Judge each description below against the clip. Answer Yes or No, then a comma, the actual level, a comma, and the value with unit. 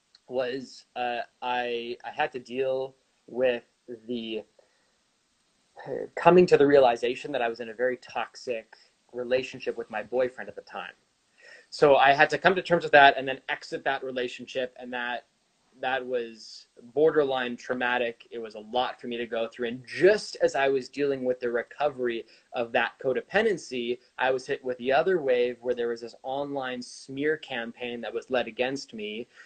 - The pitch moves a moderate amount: No, narrow, 2.2 semitones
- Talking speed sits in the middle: Yes, average, 180 wpm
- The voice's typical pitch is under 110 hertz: No, low, 125 Hz